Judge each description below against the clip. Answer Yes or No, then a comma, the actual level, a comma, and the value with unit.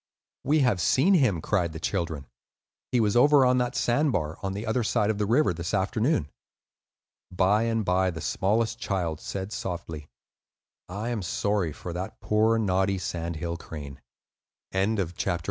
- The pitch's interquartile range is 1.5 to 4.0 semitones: No, average, 4.9 semitones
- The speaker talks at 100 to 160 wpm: No, average, 170 wpm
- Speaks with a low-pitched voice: Yes, low, 100 Hz